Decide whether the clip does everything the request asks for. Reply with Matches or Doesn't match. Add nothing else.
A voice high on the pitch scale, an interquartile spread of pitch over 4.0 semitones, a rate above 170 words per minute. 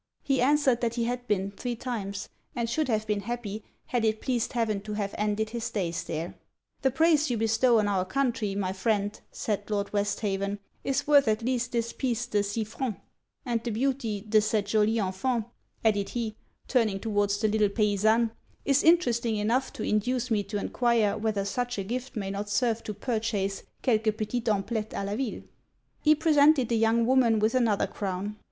Doesn't match